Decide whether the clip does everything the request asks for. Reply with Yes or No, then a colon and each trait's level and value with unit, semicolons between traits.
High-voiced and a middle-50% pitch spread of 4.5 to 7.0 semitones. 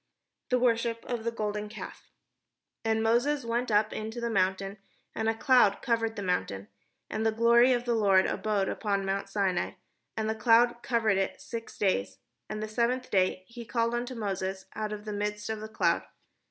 No: high, 220 Hz; average, 2.7 semitones